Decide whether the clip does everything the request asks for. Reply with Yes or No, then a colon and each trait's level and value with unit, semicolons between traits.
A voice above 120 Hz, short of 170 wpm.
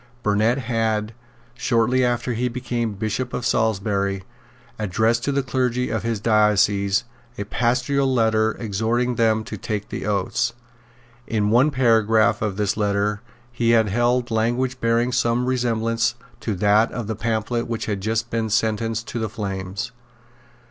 No: low, 115 Hz; average, 150 wpm